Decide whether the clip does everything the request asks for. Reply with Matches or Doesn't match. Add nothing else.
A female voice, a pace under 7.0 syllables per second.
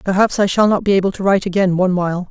Doesn't match